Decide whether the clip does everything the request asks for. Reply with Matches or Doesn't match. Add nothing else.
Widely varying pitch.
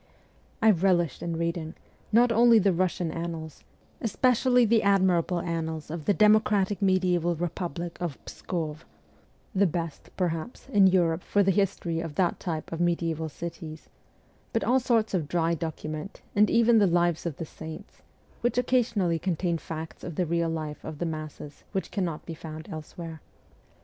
Doesn't match